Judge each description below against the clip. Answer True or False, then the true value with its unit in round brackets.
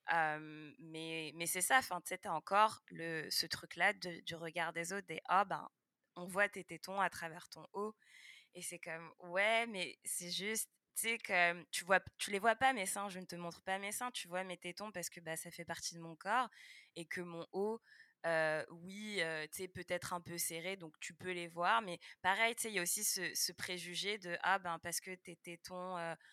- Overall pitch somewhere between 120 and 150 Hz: False (180 Hz)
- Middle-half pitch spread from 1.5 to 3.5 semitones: True (2.8 semitones)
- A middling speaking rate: False (235 wpm)